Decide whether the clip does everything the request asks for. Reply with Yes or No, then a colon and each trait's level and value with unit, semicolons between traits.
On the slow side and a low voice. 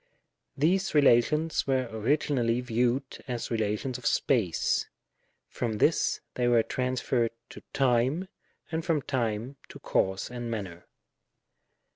Yes: slow, 115 wpm; low, 125 Hz